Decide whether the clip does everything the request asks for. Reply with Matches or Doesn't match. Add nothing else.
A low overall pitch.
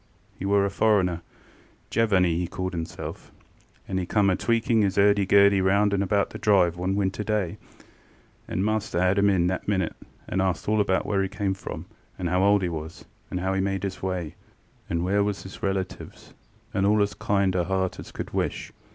Matches